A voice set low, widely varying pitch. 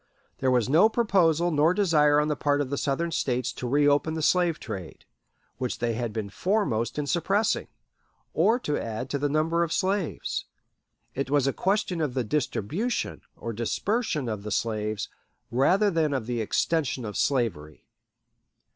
No: medium, 145 Hz; wide, 5.8 semitones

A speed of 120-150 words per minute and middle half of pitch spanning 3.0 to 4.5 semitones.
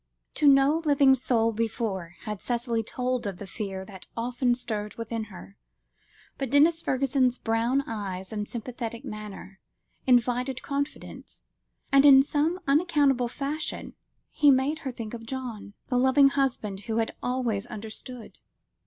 Yes: average, 140 wpm; average, 3.9 semitones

